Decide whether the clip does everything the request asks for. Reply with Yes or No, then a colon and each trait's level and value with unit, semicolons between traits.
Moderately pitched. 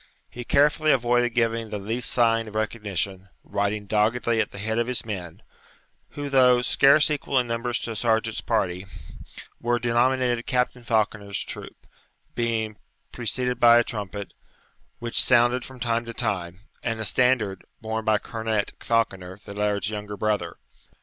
No: low, 115 Hz